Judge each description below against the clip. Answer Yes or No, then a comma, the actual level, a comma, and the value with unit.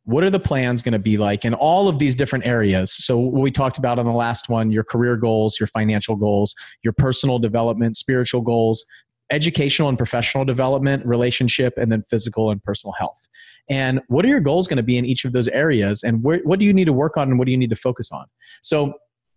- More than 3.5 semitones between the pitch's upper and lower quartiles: No, average, 3.0 semitones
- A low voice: Yes, low, 125 Hz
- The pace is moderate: No, fast, 235 wpm